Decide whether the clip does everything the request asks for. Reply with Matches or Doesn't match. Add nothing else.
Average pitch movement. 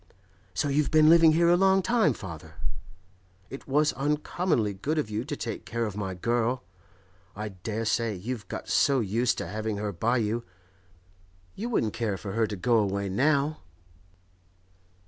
Doesn't match